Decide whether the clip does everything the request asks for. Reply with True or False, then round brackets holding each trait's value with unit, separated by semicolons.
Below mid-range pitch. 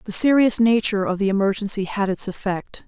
False (205 Hz)